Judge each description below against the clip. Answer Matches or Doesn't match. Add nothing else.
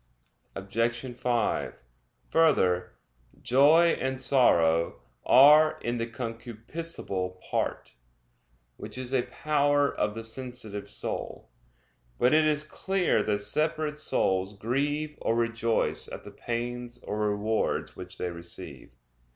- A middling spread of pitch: Doesn't match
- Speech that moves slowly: Matches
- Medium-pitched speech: Doesn't match